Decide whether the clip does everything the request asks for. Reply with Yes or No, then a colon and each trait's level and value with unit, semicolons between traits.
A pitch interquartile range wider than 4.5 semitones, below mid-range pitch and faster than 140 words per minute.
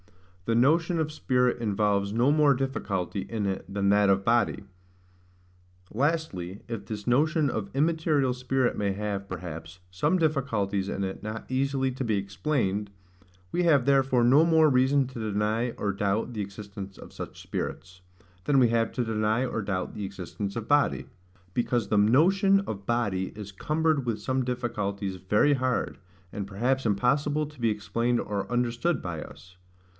Yes: average, 5.1 semitones; low, 115 Hz; average, 160 wpm